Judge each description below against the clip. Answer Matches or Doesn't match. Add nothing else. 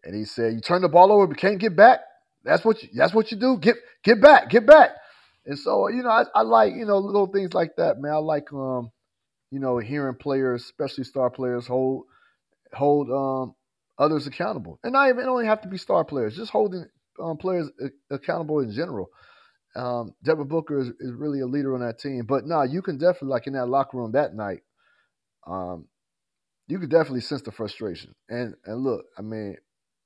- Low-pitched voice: Doesn't match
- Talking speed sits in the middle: Doesn't match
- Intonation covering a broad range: Matches